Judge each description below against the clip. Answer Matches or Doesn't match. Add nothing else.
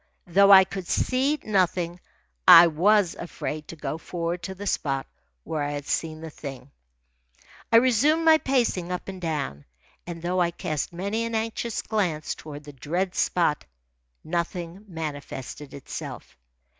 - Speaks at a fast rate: Doesn't match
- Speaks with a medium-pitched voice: Matches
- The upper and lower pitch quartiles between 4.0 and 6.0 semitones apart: Matches